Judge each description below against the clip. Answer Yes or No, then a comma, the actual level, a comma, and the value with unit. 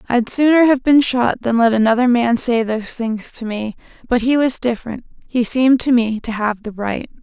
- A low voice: No, high, 240 Hz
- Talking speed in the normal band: No, fast, 215 wpm